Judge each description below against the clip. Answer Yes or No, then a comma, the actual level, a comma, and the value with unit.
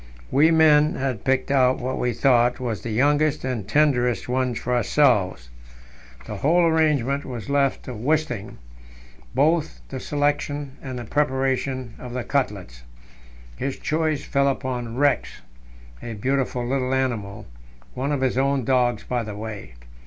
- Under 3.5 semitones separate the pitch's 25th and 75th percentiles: Yes, average, 3.0 semitones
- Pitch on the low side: Yes, low, 130 Hz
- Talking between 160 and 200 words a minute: No, average, 145 wpm